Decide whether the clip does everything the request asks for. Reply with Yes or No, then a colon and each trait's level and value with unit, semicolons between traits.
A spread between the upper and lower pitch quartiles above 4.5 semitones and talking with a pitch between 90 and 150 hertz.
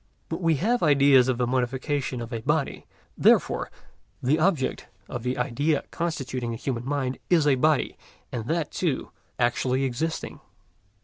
No: average, 3.7 semitones; low, 135 Hz